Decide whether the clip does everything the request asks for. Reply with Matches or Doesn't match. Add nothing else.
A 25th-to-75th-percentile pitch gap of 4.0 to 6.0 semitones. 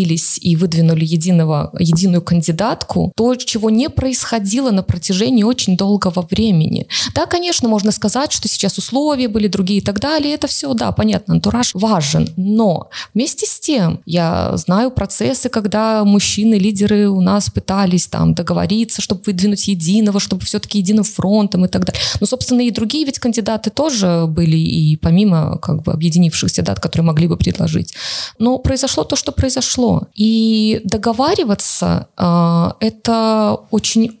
Matches